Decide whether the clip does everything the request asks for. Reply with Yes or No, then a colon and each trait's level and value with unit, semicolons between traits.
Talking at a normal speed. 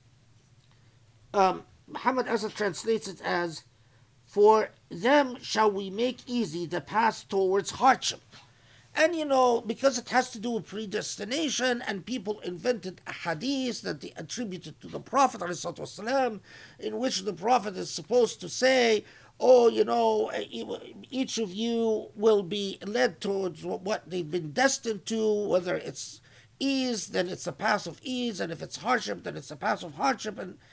Yes: average, 155 wpm